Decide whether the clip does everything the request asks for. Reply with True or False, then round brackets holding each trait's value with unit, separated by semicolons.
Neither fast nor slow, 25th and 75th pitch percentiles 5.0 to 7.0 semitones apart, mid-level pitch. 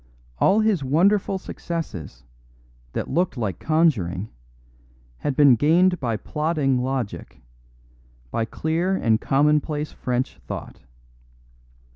False (100 wpm; 5.4 semitones; 150 Hz)